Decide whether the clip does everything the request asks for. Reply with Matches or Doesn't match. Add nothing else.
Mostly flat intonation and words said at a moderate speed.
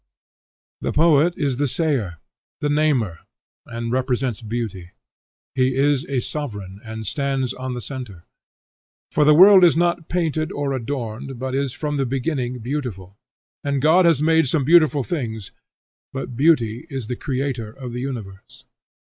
Doesn't match